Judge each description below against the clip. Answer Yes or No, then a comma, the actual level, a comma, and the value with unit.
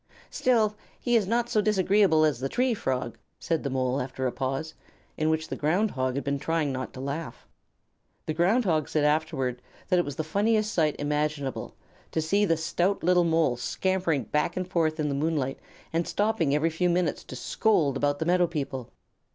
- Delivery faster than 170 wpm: Yes, average, 195 wpm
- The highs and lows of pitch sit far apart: No, average, 4.5 semitones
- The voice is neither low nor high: Yes, medium, 160 Hz